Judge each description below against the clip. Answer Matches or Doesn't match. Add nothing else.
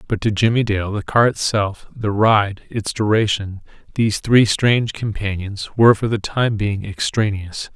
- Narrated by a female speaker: Doesn't match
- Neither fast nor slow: Matches